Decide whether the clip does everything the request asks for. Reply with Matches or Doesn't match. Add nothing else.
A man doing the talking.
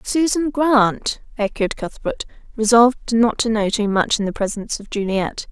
Doesn't match